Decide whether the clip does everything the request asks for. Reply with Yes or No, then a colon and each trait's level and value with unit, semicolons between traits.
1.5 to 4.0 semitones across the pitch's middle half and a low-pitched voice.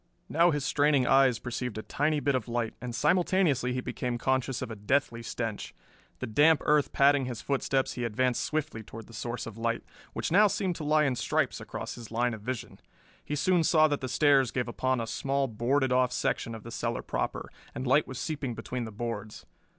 Yes: average, 3.6 semitones; low, 130 Hz